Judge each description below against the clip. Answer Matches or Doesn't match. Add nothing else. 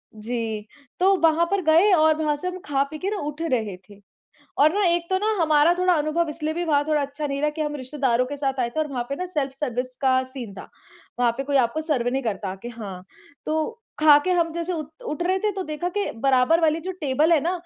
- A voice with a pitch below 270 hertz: Doesn't match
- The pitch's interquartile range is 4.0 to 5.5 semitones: Matches